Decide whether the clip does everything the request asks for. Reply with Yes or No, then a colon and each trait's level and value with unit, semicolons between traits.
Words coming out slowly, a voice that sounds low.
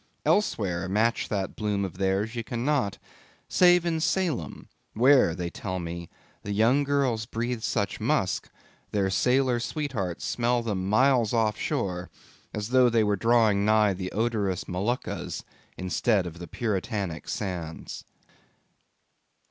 Yes: slow, 130 wpm; low, 110 Hz